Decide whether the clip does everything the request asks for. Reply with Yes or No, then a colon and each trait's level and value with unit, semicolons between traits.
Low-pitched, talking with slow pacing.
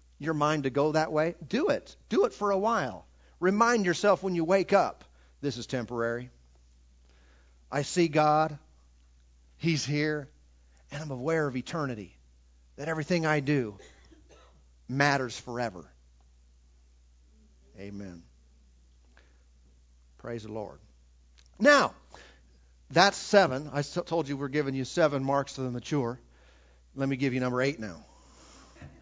Yes: low, 115 Hz; slow, 130 wpm